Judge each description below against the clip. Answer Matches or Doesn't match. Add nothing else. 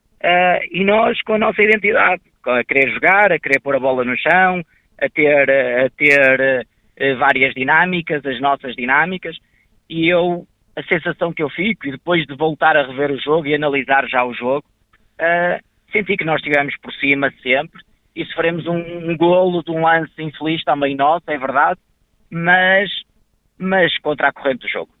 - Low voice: Doesn't match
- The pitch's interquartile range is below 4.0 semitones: Doesn't match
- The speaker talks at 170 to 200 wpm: Matches